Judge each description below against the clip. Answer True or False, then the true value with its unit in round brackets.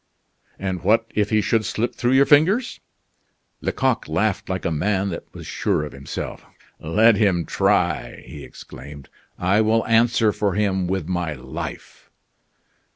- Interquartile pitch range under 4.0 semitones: False (4.4 semitones)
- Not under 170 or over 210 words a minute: False (150 wpm)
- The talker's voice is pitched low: True (100 Hz)